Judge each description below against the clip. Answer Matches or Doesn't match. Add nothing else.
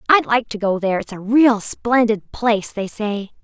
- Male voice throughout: Doesn't match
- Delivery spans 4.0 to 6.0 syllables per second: Matches